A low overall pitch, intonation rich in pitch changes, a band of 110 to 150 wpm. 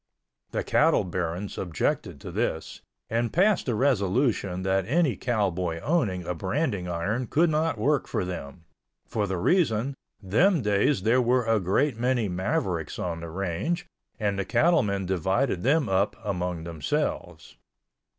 Yes: low, 100 Hz; wide, 6.1 semitones; average, 140 wpm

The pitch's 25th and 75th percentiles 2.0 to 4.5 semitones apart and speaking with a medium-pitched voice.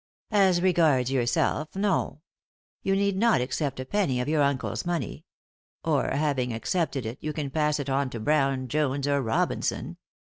Yes: average, 4.1 semitones; medium, 145 Hz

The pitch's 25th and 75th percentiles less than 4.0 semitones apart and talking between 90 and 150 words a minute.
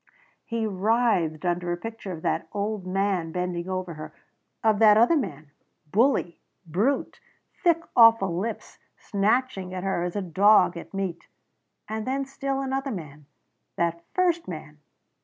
No: average, 4.8 semitones; average, 145 wpm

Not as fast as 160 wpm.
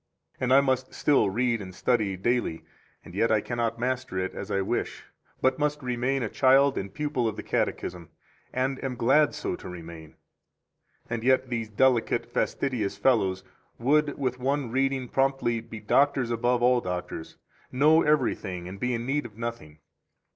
No: average, 170 wpm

